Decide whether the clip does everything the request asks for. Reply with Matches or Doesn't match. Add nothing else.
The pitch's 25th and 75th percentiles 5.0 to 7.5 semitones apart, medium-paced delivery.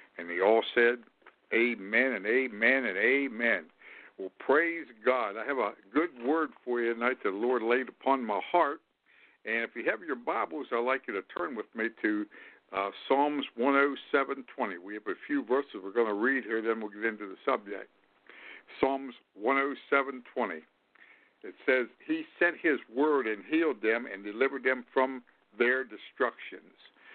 Matches